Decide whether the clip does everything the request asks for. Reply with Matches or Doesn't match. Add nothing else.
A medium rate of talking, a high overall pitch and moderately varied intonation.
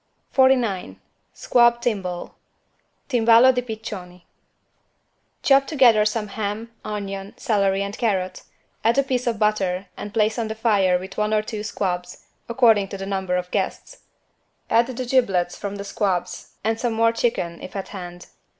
Matches